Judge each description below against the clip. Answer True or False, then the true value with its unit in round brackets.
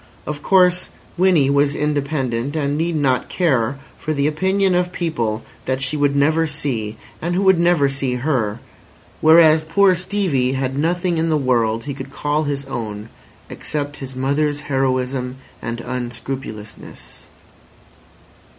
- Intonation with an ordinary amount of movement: True (3.8 semitones)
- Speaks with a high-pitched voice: False (145 Hz)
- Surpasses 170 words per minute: False (140 wpm)